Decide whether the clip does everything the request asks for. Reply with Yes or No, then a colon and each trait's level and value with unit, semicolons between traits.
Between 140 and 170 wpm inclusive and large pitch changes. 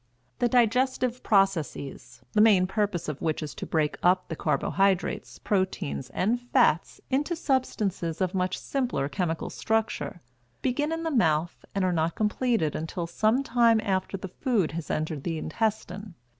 Yes: average, 155 wpm; wide, 5.9 semitones